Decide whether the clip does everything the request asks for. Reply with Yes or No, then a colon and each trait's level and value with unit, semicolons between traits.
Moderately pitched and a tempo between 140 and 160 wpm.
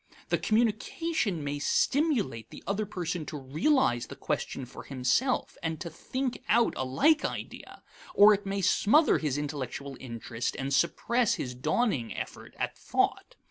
Yes: medium, 170 Hz; average, 150 wpm